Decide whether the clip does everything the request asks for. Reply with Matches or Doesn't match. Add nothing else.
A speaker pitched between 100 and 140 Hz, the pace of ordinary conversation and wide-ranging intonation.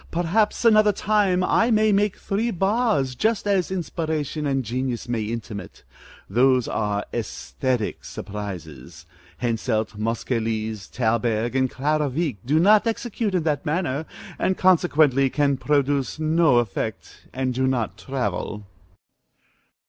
Doesn't match